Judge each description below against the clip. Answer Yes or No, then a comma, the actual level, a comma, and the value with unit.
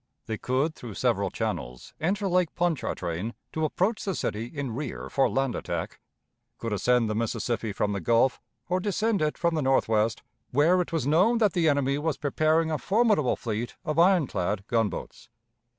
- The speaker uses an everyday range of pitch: No, wide, 6.8 semitones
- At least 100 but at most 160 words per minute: No, average, 175 wpm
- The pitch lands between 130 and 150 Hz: Yes, medium, 140 Hz